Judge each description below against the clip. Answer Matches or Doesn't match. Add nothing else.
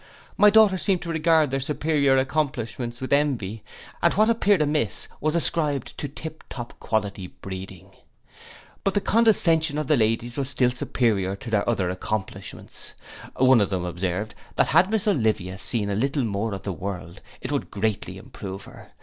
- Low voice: Matches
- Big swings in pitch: Matches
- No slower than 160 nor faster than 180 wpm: Matches